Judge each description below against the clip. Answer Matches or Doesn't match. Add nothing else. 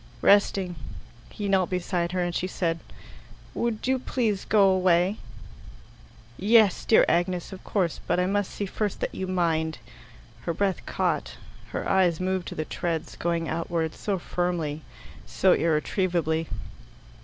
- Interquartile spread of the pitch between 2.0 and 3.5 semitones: Matches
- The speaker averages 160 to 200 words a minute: Doesn't match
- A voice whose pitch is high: Doesn't match